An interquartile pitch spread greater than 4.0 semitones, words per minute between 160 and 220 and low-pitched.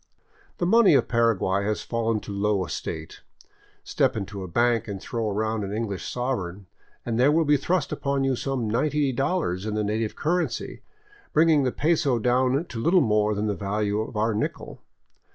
Yes: average, 4.7 semitones; average, 170 wpm; low, 115 Hz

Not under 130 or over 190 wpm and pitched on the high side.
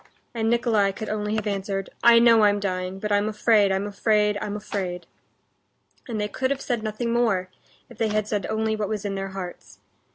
No: average, 200 wpm; high, 210 Hz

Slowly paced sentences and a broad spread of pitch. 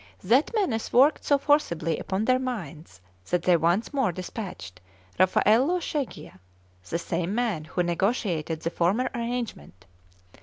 Yes: slow, 130 wpm; wide, 7.0 semitones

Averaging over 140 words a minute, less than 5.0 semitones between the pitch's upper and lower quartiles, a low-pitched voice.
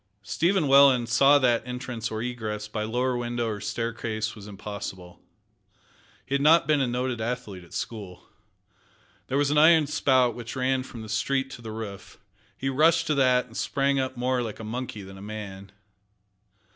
Yes: average, 175 wpm; average, 3.7 semitones; low, 120 Hz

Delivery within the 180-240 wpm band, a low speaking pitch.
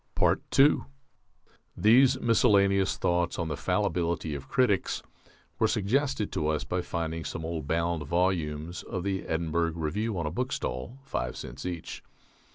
No: average, 140 wpm; very low, 85 Hz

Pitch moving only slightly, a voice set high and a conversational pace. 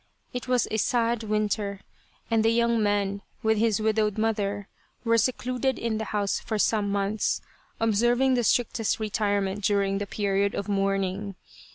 Yes: narrow, 2.3 semitones; high, 215 Hz; average, 155 wpm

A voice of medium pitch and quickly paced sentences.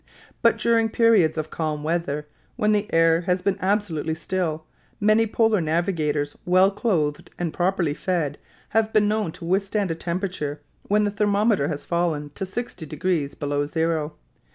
No: medium, 175 Hz; average, 155 wpm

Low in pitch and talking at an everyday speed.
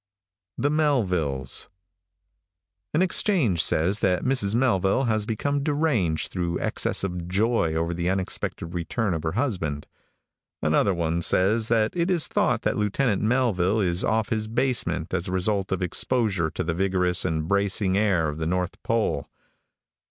Yes: very low, 95 Hz; average, 150 wpm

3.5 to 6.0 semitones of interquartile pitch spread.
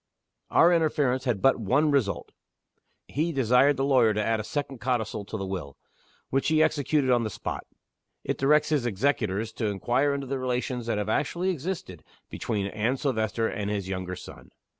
Yes: average, 4.8 semitones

